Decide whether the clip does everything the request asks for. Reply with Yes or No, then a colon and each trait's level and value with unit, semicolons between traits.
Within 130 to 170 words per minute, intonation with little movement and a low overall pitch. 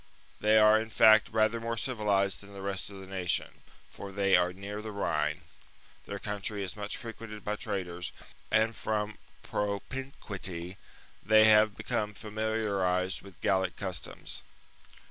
Yes: average, 145 wpm; narrow, 2.1 semitones; low, 105 Hz